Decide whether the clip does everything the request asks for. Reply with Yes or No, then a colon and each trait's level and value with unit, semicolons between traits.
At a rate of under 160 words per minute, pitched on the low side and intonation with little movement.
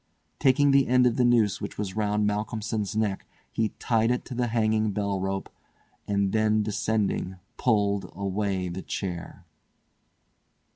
Yes: average, 145 wpm; low, 105 Hz; narrow, 2.1 semitones